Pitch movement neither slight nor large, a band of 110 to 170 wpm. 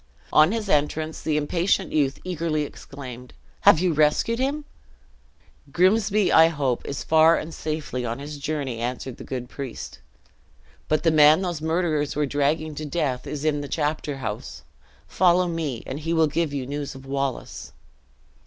Yes: average, 3.0 semitones; average, 160 wpm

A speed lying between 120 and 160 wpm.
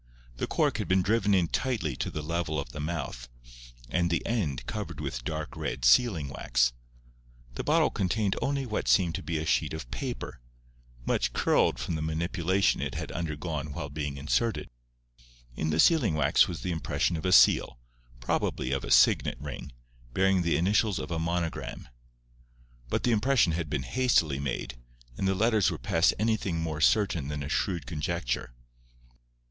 No: average, 170 wpm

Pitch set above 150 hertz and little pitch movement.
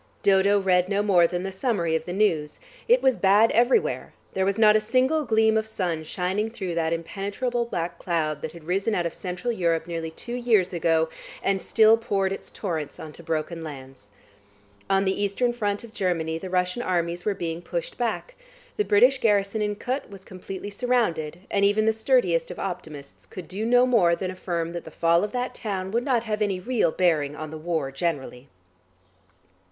No: high, 190 Hz; average, 4.6 semitones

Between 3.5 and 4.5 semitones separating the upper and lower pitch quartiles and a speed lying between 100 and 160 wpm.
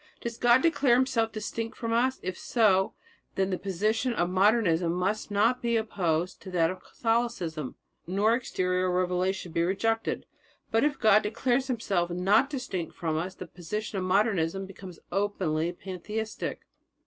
Yes: average, 4.0 semitones; average, 150 wpm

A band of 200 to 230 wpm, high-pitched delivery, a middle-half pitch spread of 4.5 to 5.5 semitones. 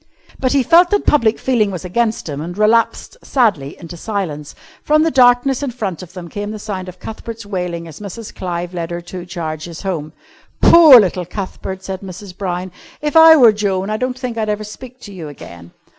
Yes: fast, 205 wpm; high, 200 Hz; average, 5.2 semitones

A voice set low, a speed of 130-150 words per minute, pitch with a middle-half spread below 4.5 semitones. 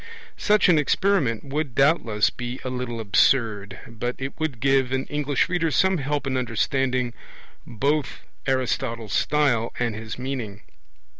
Yes: low, 130 Hz; average, 140 wpm; average, 3.8 semitones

